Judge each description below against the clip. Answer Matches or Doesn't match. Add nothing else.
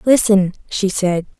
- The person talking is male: Doesn't match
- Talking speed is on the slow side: Matches